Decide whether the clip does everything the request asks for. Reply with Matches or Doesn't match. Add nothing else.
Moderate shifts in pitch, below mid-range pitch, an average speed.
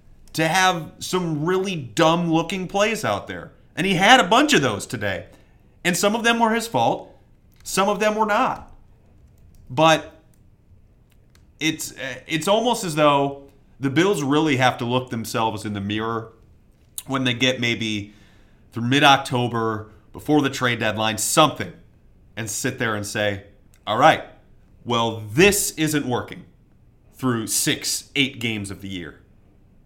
Doesn't match